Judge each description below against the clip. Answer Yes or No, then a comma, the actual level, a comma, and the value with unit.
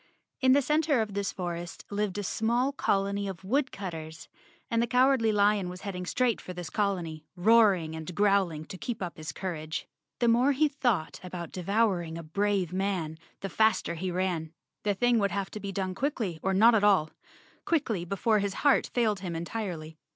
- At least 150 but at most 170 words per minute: No, average, 195 wpm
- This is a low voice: No, high, 195 Hz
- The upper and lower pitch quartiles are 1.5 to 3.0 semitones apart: No, average, 4.4 semitones